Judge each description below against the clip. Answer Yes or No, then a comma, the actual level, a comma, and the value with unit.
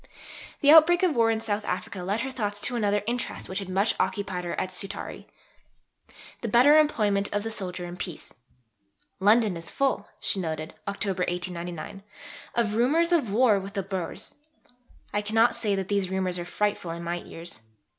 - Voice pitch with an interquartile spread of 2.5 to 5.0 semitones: Yes, average, 3.8 semitones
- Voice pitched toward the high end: Yes, high, 205 Hz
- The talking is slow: No, average, 175 wpm